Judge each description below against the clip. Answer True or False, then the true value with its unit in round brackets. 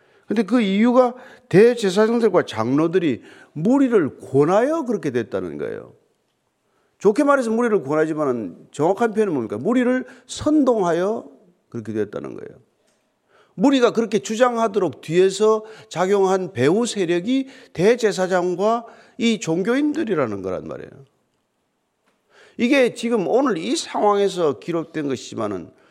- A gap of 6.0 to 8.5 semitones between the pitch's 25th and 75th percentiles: False (5.6 semitones)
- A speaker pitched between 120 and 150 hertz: False (220 Hz)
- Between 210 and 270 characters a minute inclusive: False (300 characters per minute)